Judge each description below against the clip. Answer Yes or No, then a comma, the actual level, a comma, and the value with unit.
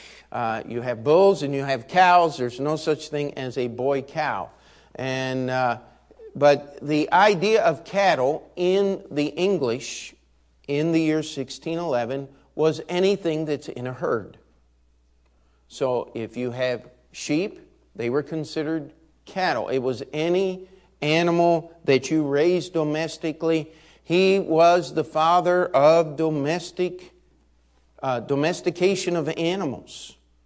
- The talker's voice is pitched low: No, medium, 155 Hz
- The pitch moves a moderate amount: Yes, average, 4.7 semitones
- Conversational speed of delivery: No, slow, 130 wpm